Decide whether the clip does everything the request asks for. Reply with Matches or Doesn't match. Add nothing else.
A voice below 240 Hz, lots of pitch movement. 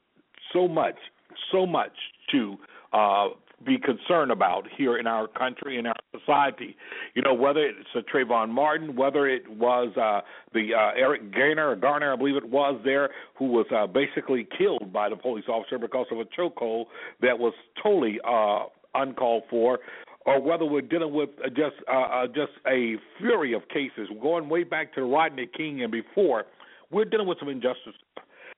Matches